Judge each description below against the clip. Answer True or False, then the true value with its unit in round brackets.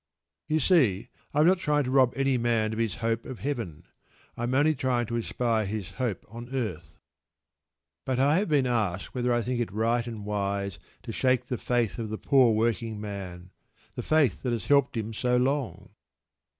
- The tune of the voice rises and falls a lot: False (3.3 semitones)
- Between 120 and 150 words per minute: False (195 wpm)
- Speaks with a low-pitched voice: True (120 Hz)